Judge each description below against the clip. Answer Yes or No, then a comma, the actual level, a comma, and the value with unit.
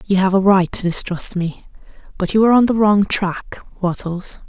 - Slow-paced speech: No, average, 200 wpm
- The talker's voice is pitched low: No, high, 190 Hz